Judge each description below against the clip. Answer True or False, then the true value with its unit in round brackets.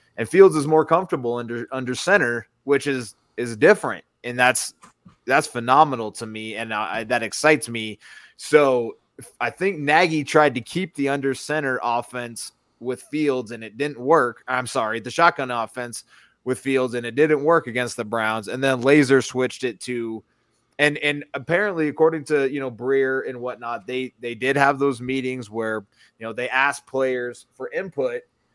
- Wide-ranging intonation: False (3.5 semitones)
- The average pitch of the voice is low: True (130 Hz)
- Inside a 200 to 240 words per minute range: False (175 wpm)